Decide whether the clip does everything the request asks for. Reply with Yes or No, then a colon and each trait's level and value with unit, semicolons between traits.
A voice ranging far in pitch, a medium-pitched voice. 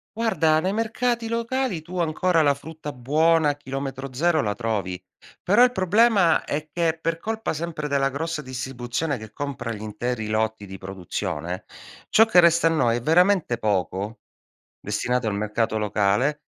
Yes: wide, 7.3 semitones; medium, 145 Hz